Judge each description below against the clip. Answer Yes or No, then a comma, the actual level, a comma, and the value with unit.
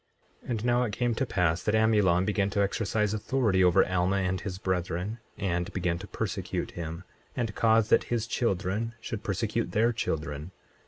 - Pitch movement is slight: No, average, 3.7 semitones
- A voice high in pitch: No, low, 100 Hz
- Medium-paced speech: Yes, average, 175 wpm